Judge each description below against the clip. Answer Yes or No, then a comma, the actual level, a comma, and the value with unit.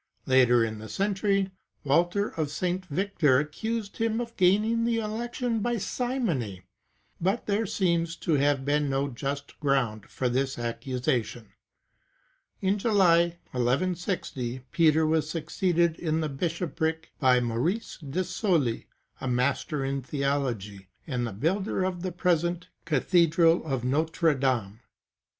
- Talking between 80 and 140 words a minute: Yes, slow, 135 wpm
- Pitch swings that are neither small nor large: No, wide, 6.0 semitones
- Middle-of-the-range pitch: Yes, medium, 160 Hz